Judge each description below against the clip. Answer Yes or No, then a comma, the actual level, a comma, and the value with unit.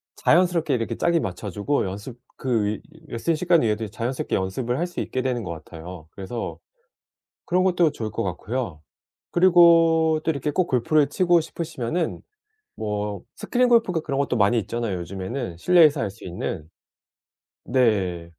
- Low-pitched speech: Yes, low, 125 Hz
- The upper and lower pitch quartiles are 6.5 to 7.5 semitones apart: No, wide, 8.3 semitones